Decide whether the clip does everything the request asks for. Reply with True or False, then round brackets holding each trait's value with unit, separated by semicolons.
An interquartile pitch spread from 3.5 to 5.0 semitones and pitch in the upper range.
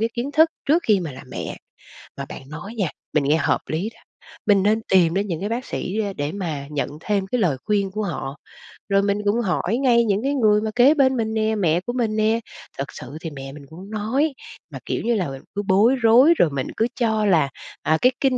False (5.5 semitones; 210 Hz)